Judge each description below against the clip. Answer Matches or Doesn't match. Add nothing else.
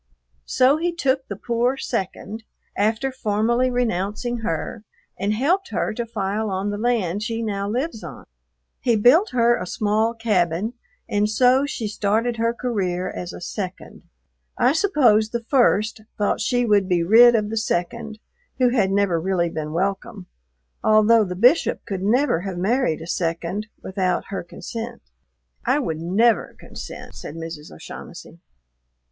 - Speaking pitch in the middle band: Doesn't match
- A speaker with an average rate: Matches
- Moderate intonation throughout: Matches